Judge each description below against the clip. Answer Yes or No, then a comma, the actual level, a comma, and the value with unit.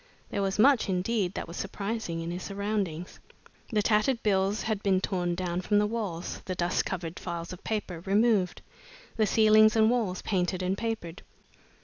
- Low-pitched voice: No, high, 195 Hz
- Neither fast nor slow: Yes, average, 170 wpm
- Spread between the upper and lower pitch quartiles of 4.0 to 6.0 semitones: No, average, 3.2 semitones